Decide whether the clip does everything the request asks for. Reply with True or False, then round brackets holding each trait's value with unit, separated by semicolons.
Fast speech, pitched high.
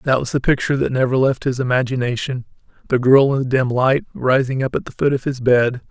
False (225 wpm; 130 Hz)